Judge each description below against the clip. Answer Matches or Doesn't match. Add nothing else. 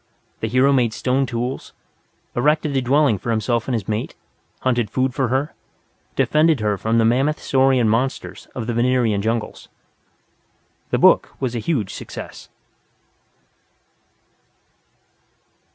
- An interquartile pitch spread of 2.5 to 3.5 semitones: Matches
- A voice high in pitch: Doesn't match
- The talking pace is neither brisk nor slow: Doesn't match